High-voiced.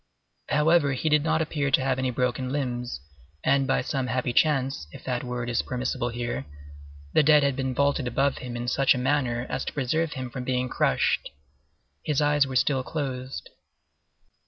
No: low, 130 Hz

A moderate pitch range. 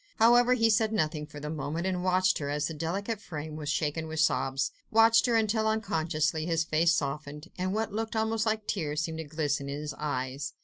No: wide, 6.3 semitones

